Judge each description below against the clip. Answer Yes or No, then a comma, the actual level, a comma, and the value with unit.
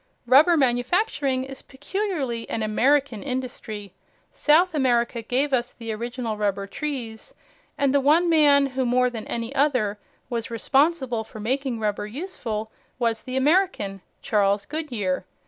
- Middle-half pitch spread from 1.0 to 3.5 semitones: No, average, 4.2 semitones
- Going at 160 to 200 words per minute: No, slow, 135 wpm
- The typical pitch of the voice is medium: No, very high, 255 Hz